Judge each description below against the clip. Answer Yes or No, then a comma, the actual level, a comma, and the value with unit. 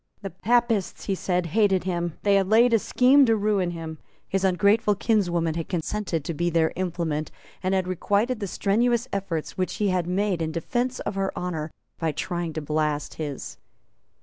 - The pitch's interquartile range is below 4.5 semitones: Yes, average, 3.8 semitones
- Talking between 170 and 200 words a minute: Yes, average, 180 wpm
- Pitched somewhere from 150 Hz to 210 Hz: Yes, medium, 185 Hz